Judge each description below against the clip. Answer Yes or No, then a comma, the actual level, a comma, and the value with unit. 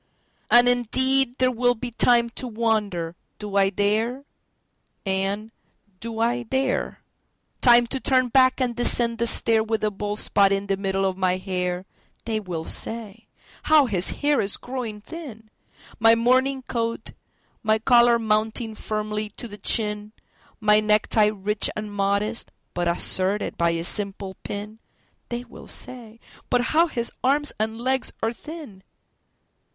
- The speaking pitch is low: No, high, 220 Hz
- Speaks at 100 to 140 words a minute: Yes, slow, 135 wpm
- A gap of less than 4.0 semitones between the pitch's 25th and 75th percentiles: Yes, average, 3.0 semitones